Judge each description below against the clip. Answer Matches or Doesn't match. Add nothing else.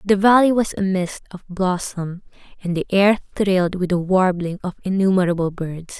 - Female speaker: Matches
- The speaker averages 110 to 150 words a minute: Doesn't match